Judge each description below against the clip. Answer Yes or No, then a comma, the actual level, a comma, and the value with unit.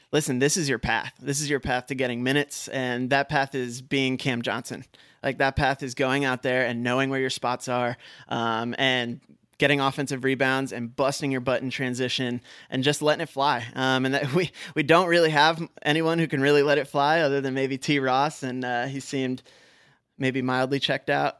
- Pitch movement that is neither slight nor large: No, narrow, 1.9 semitones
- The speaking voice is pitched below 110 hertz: No, low, 135 Hz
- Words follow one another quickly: Yes, fast, 215 wpm